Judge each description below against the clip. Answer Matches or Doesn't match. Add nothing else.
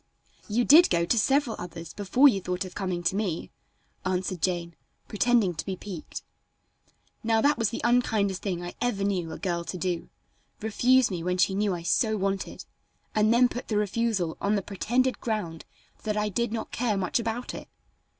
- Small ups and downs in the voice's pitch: Doesn't match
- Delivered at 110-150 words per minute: Doesn't match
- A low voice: Doesn't match